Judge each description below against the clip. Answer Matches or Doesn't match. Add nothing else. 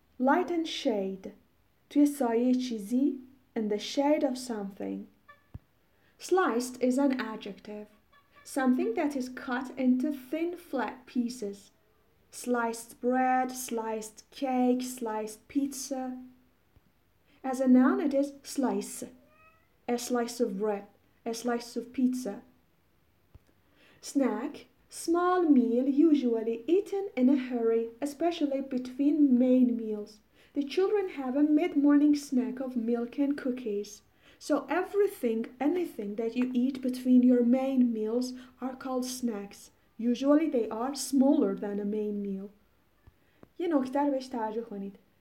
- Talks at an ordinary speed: Matches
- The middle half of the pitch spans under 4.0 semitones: Matches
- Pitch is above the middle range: Matches